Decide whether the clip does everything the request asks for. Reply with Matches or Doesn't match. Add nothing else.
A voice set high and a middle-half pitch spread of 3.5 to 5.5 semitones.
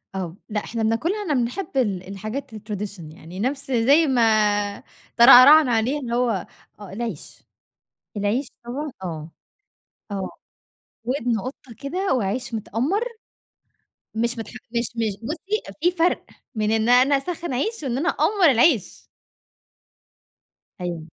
Matches